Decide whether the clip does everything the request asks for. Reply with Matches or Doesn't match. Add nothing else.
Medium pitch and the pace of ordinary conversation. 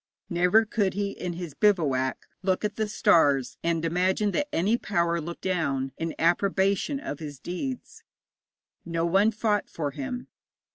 Matches